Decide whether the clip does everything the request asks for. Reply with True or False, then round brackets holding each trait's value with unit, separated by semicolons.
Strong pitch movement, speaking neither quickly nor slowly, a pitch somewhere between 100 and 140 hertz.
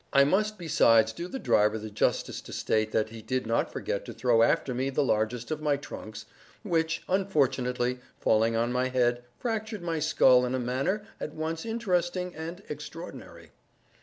True (6.2 semitones; 175 wpm; 135 Hz)